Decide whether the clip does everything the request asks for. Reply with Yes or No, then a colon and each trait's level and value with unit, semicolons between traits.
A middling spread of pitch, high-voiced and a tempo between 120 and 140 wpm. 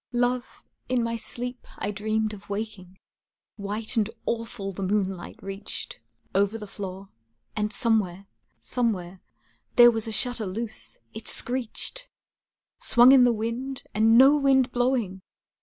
Yes: average, 3.3 semitones; high, 220 Hz; slow, 135 wpm